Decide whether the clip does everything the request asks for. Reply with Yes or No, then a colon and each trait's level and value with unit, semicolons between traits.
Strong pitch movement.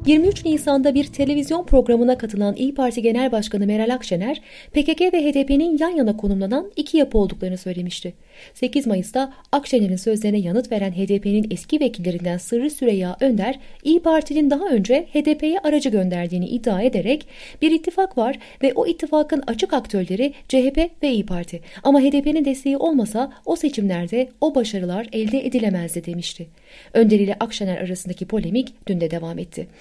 Yes: wide, 6.1 semitones